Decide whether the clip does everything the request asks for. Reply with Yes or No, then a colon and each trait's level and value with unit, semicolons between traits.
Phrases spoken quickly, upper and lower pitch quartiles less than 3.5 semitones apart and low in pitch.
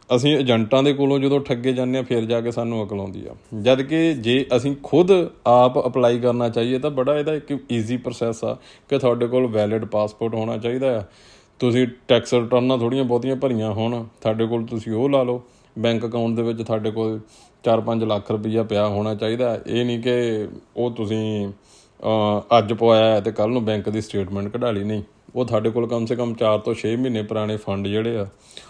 Yes: fast, 190 wpm; narrow, 2.4 semitones; low, 115 Hz